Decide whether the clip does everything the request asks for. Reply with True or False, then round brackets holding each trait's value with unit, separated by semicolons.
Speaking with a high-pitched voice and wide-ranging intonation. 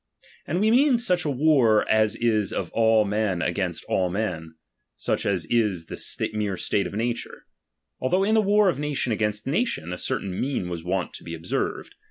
False (110 Hz; 7.9 semitones)